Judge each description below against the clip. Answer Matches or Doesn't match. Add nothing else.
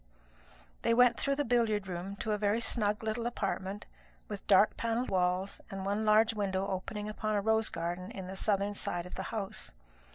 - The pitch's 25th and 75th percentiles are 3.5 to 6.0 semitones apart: Doesn't match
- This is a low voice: Doesn't match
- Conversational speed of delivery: Matches